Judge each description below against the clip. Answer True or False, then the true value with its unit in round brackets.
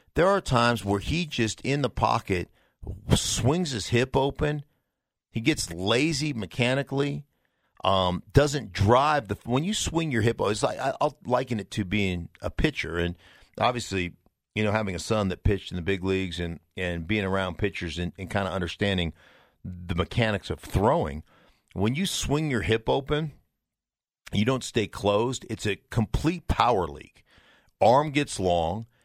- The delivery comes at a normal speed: True (165 wpm)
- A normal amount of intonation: False (5.7 semitones)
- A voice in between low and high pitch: False (110 Hz)